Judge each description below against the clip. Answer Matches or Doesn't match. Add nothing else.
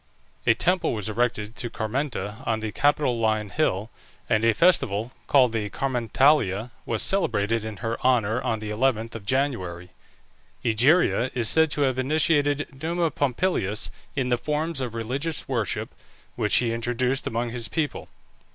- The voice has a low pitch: Matches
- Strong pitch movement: Doesn't match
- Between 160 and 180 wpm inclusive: Doesn't match